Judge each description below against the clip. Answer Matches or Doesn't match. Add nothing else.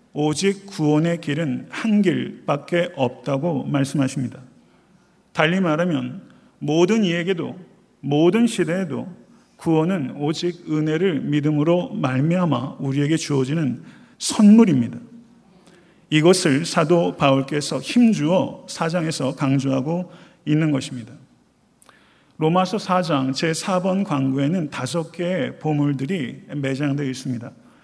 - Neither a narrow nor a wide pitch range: Matches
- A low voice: Doesn't match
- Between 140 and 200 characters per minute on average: Doesn't match